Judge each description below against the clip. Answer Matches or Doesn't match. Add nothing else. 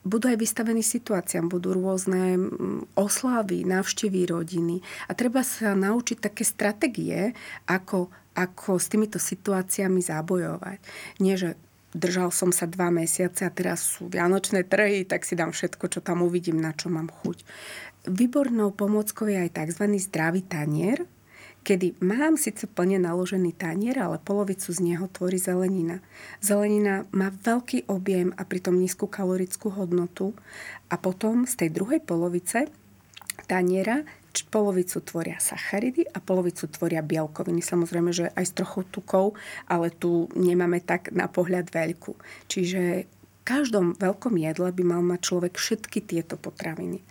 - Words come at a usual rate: Matches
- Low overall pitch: Doesn't match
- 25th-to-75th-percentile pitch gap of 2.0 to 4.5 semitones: Matches